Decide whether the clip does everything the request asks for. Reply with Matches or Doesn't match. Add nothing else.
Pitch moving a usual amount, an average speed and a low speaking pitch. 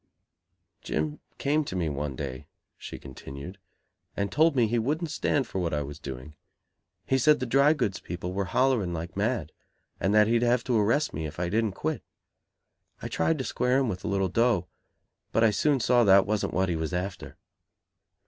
Doesn't match